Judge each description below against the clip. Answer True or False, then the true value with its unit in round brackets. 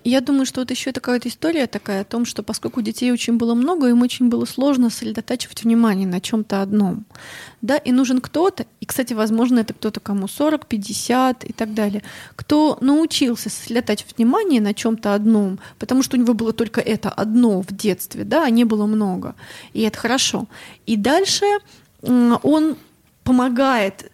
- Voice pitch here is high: True (235 Hz)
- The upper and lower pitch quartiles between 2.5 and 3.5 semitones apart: True (3.2 semitones)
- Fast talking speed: True (170 wpm)